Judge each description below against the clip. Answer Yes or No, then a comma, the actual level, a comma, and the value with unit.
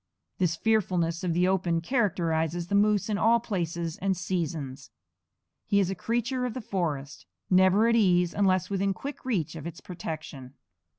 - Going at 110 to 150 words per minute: No, average, 165 wpm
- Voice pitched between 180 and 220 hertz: Yes, medium, 185 Hz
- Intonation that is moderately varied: Yes, average, 3.6 semitones